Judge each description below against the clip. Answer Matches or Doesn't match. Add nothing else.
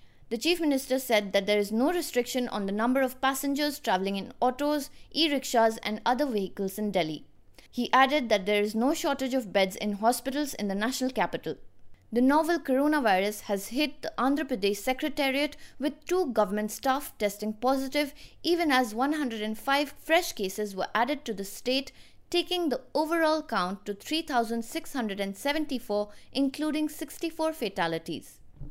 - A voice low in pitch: Doesn't match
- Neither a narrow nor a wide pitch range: Doesn't match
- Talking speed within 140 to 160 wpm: Matches